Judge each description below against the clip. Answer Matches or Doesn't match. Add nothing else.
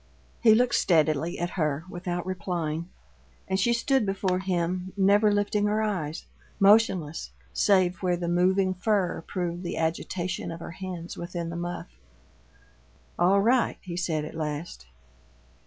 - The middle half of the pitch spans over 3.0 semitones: Doesn't match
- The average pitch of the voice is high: Doesn't match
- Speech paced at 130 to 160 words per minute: Matches